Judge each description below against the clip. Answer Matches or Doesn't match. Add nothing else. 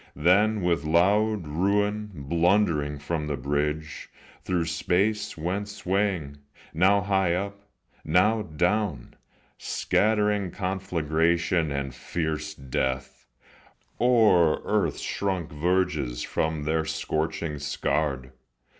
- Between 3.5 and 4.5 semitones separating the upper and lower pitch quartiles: Doesn't match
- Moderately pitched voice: Doesn't match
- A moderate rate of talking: Doesn't match